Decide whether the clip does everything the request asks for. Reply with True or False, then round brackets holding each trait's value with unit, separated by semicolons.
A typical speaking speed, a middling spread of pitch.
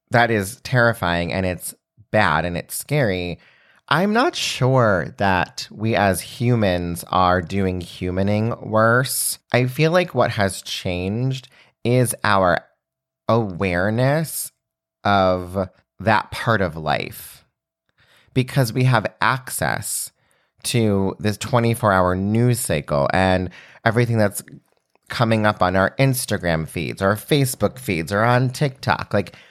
False (120 wpm; 4.8 semitones)